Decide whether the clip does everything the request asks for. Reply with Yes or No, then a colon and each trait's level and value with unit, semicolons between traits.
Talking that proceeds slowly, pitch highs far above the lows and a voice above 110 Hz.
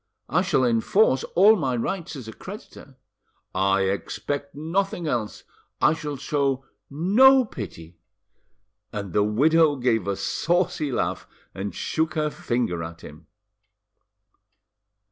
Yes: slow, 125 wpm; wide, 7.5 semitones; medium, 140 Hz